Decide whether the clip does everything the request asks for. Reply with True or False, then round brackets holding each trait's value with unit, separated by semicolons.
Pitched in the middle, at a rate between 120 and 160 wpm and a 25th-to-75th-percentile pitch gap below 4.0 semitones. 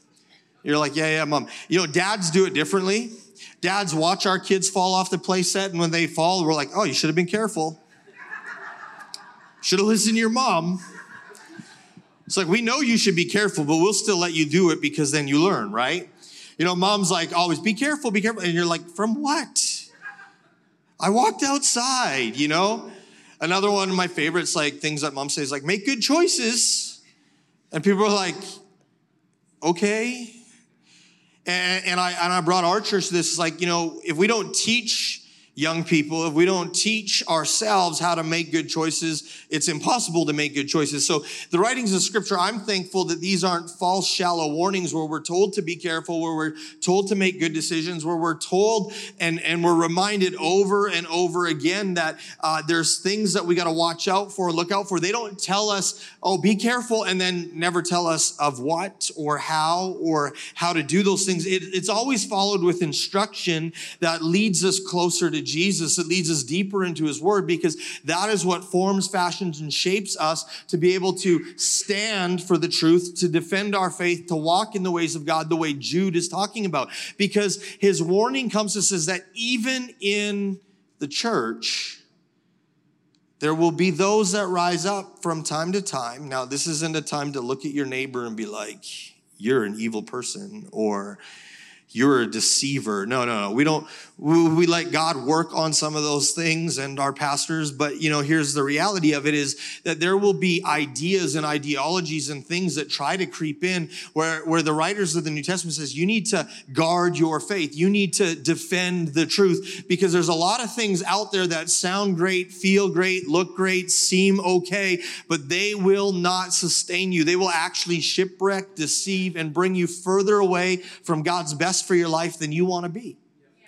False (175 Hz; 195 wpm; 3.2 semitones)